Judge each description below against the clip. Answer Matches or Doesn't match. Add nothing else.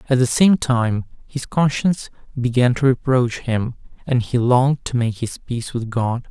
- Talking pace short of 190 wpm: Matches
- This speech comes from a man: Matches